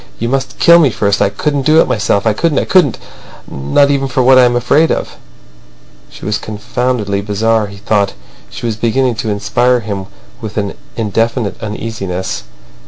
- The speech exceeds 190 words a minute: No, average, 170 wpm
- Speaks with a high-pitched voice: No, low, 115 Hz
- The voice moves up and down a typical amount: Yes, average, 3.9 semitones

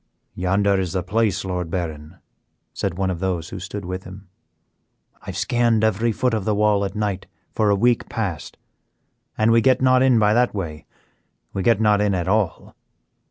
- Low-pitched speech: Yes, low, 100 Hz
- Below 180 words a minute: No, average, 190 wpm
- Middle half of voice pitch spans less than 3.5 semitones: Yes, average, 3.0 semitones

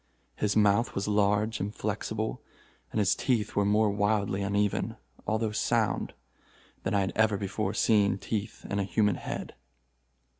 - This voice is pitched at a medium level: No, low, 105 Hz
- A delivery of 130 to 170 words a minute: Yes, average, 150 wpm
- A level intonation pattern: Yes, narrow, 1.4 semitones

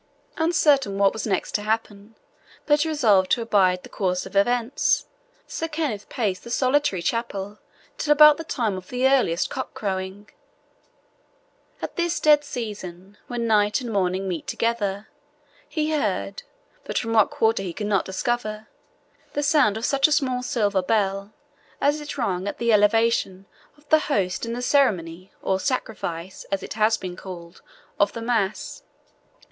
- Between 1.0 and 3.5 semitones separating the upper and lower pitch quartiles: No, average, 4.8 semitones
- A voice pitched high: Yes, high, 215 Hz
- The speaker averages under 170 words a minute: Yes, average, 160 wpm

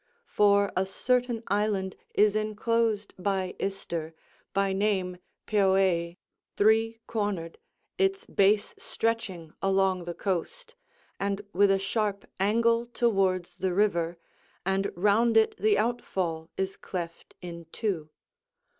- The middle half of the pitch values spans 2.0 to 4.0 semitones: Yes, average, 2.8 semitones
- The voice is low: No, high, 200 Hz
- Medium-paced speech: No, slow, 115 wpm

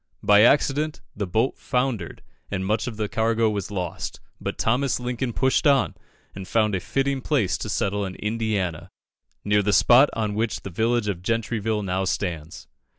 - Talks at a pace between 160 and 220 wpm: Yes, average, 170 wpm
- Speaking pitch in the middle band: No, low, 110 Hz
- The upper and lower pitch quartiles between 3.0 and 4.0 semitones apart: Yes, average, 3.6 semitones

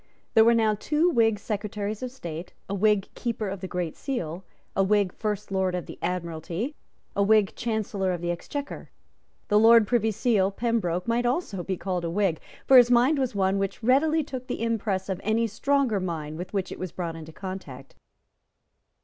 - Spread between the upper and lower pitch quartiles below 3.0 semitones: No, average, 4.1 semitones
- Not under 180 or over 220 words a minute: Yes, average, 190 wpm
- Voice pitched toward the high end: Yes, high, 205 Hz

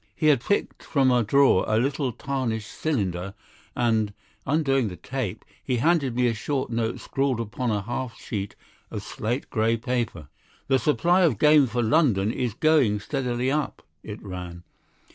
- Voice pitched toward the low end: Yes, low, 120 Hz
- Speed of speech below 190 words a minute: Yes, average, 160 wpm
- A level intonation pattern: No, average, 4.1 semitones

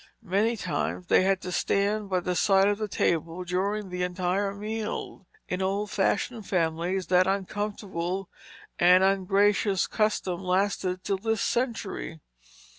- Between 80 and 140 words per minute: Yes, slow, 135 wpm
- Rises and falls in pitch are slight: Yes, narrow, 2.2 semitones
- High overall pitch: Yes, high, 195 Hz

